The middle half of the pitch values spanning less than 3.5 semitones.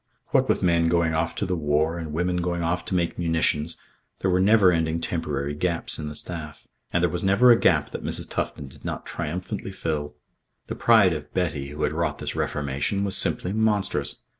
Yes: average, 3.0 semitones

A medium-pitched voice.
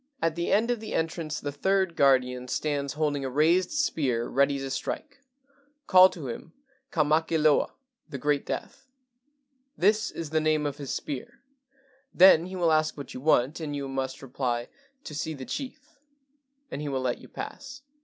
Yes: medium, 155 Hz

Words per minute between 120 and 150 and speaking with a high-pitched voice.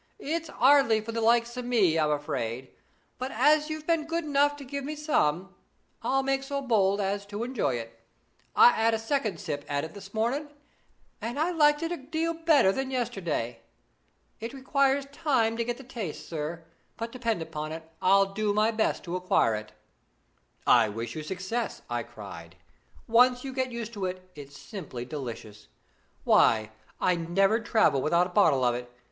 No: average, 180 wpm; high, 220 Hz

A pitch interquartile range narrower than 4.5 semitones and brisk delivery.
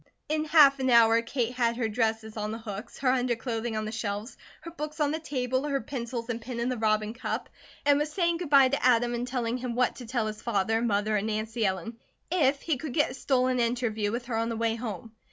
Yes: average, 2.9 semitones; fast, 235 wpm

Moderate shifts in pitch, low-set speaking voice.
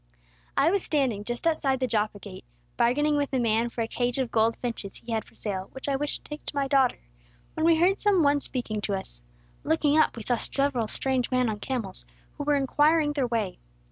No: average, 4.5 semitones; very high, 255 Hz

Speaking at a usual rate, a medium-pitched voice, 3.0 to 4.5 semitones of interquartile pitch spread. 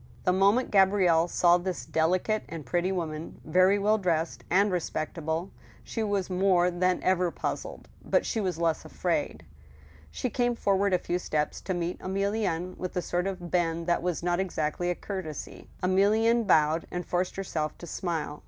No: average, 170 wpm; medium, 180 Hz; narrow, 2.5 semitones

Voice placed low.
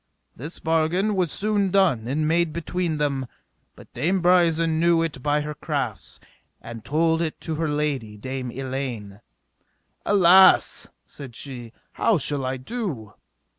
No: medium, 155 Hz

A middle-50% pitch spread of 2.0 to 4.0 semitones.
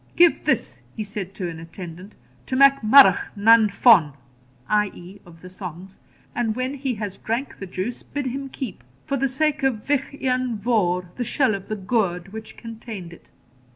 No: wide, 5.4 semitones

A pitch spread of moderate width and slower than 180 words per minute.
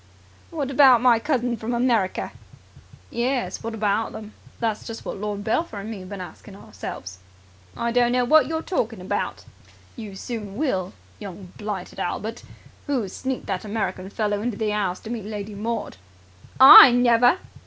Yes: average, 3.3 semitones; average, 165 wpm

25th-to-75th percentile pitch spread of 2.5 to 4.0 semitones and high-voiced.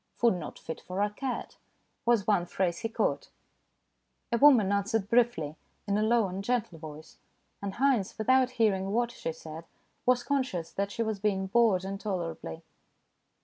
No: average, 4.4 semitones; high, 205 Hz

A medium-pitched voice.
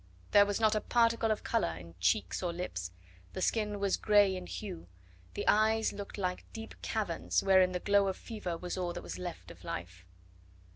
No: high, 195 Hz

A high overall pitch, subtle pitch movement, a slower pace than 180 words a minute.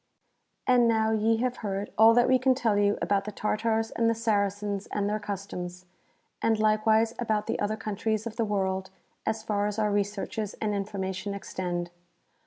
No: high, 210 Hz; narrow, 1.8 semitones; average, 185 wpm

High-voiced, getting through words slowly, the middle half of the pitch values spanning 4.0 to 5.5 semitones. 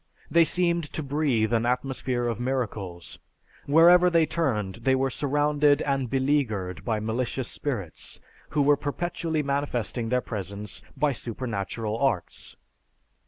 No: low, 130 Hz; slow, 125 wpm; average, 4.7 semitones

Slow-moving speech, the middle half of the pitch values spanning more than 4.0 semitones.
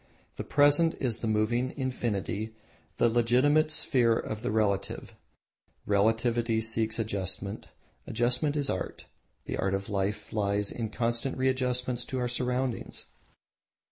No: slow, 130 wpm; average, 2.9 semitones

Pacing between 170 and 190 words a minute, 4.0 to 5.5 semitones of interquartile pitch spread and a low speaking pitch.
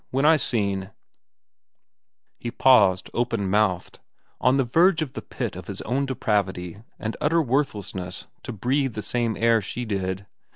No: average, 155 wpm; average, 5.0 semitones; low, 115 Hz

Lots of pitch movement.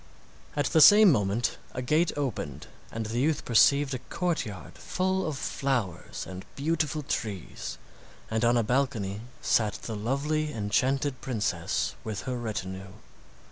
Yes: wide, 5.9 semitones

